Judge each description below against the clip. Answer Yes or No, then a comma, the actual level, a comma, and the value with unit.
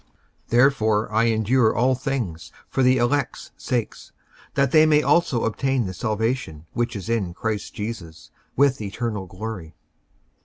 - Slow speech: No, average, 145 wpm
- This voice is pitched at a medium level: No, low, 115 Hz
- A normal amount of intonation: Yes, average, 3.8 semitones